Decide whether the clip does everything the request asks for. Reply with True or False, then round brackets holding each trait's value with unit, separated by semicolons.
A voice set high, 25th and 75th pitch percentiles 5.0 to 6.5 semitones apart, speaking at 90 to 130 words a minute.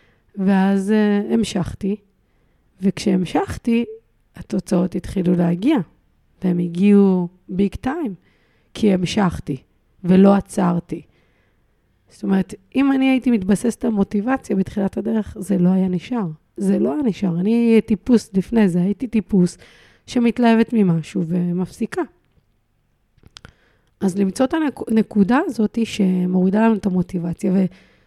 False (195 Hz; 3.6 semitones; 110 wpm)